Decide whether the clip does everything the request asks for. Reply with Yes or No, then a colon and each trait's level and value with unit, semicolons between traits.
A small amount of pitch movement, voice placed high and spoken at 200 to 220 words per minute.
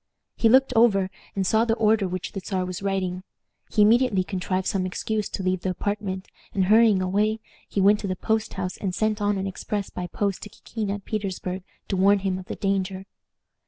Yes: narrow, 2.3 semitones; high, 195 Hz; fast, 205 wpm